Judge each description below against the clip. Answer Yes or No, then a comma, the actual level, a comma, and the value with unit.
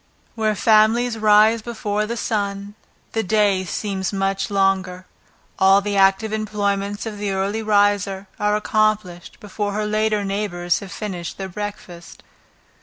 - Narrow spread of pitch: Yes, narrow, 1.7 semitones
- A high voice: Yes, high, 205 Hz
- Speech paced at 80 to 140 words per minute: Yes, slow, 135 wpm